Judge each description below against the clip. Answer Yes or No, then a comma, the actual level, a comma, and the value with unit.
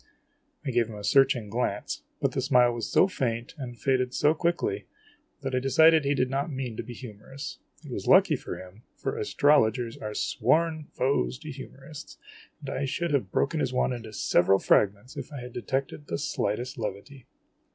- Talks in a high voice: No, low, 130 Hz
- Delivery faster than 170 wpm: Yes, average, 185 wpm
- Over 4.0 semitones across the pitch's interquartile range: No, average, 3.5 semitones